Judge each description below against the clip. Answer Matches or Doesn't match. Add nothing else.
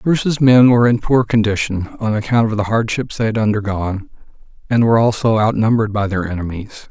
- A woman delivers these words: Doesn't match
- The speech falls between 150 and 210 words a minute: Matches